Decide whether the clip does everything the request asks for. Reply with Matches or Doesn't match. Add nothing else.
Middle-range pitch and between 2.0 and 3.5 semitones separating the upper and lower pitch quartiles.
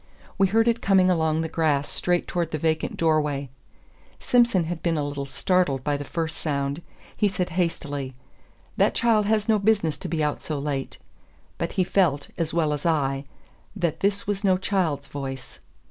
Doesn't match